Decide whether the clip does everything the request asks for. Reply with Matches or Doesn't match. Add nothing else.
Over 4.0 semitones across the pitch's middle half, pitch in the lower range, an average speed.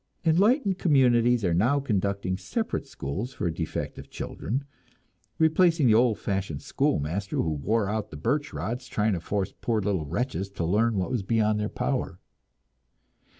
Matches